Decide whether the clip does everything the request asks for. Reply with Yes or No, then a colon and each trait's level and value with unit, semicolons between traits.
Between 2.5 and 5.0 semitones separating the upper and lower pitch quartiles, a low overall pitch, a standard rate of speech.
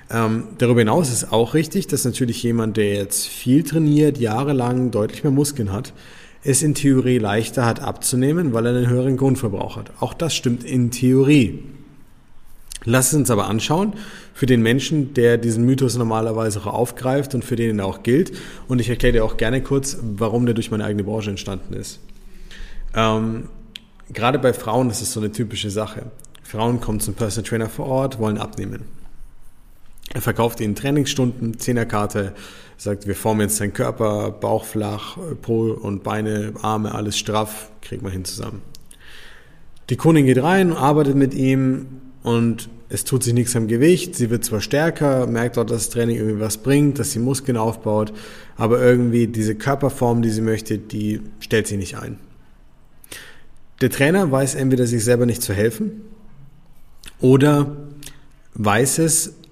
Yes: average, 3.7 semitones; low, 120 Hz; average, 170 wpm